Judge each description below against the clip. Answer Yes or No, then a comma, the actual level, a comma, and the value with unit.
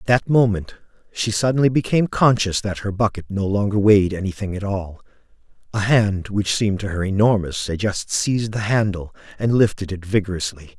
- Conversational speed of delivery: Yes, average, 180 wpm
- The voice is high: No, low, 100 Hz